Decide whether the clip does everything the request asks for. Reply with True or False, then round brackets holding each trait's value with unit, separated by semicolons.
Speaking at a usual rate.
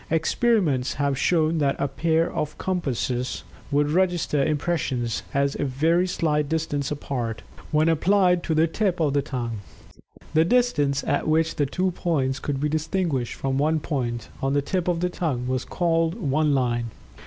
True (165 wpm)